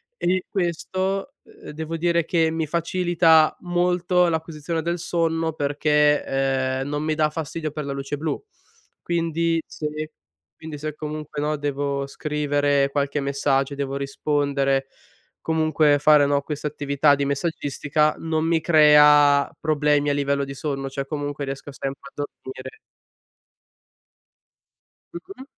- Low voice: No, medium, 150 Hz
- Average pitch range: No, narrow, 2.3 semitones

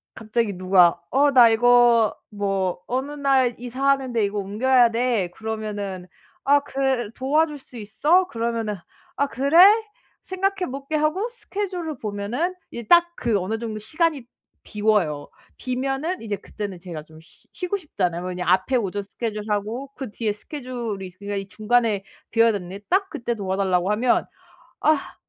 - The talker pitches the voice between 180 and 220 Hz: No, high, 230 Hz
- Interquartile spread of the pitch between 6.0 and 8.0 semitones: No, average, 5.2 semitones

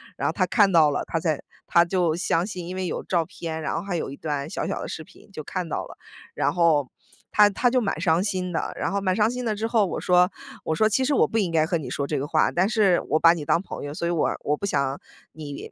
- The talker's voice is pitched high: No, medium, 175 Hz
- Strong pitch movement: No, average, 4.0 semitones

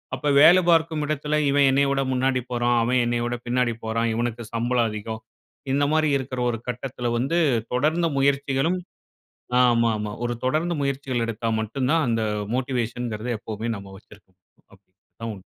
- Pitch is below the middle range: Yes, low, 125 Hz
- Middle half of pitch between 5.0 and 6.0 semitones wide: No, average, 3.2 semitones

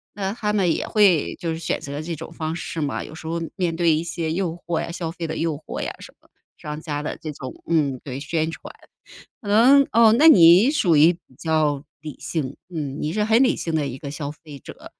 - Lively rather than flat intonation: No, average, 3.0 semitones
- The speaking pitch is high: No, medium, 165 Hz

